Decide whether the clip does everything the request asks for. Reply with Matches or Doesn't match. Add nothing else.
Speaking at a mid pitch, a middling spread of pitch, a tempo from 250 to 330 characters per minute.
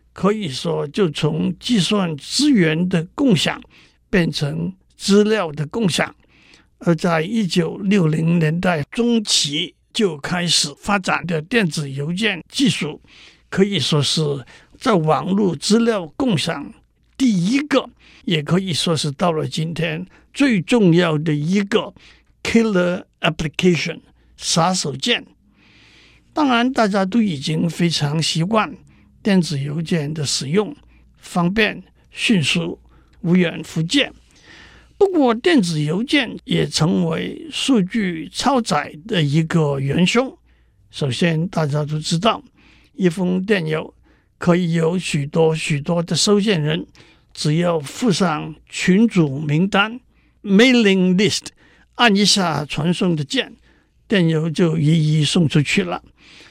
Doesn't match